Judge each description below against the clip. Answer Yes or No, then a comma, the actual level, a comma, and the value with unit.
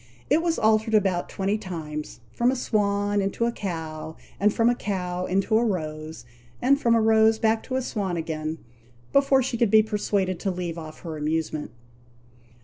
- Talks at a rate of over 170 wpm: Yes, average, 180 wpm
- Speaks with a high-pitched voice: Yes, high, 200 Hz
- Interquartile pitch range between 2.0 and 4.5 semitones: No, average, 5.1 semitones